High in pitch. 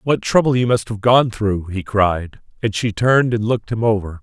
No: low, 110 Hz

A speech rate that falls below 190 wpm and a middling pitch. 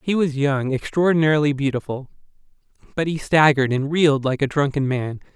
Yes: average, 155 wpm; medium, 145 Hz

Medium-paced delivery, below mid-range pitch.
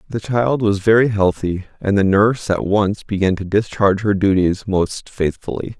Yes: average, 175 wpm; low, 100 Hz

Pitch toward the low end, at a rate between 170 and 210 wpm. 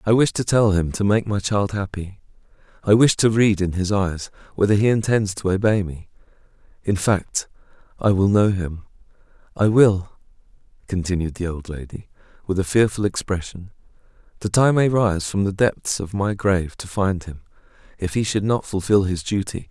Yes: low, 100 Hz; average, 175 wpm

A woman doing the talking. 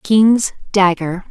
Yes: female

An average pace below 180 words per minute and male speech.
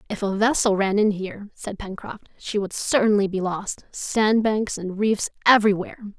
No: average, 165 wpm; female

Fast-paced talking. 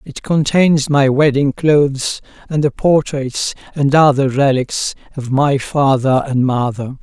No: slow, 135 wpm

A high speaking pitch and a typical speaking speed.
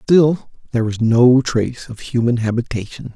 No: low, 120 Hz; average, 150 wpm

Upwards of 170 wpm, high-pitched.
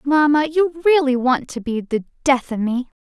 Yes: average, 200 wpm; very high, 275 Hz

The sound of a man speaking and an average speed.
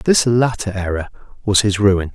Yes: male; average, 170 wpm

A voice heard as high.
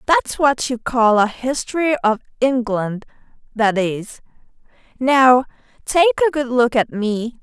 Yes: high, 245 Hz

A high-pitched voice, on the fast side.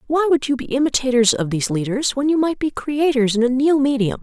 Yes: very high, 265 Hz; fast, 240 wpm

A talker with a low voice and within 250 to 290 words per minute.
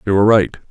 Yes: low, 100 Hz; fast, 255 wpm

